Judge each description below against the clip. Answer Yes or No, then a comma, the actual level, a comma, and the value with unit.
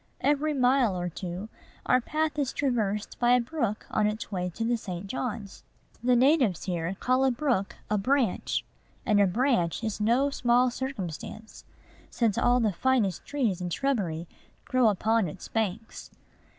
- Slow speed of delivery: No, average, 160 wpm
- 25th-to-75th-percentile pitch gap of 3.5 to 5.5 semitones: Yes, average, 4.7 semitones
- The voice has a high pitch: Yes, high, 225 Hz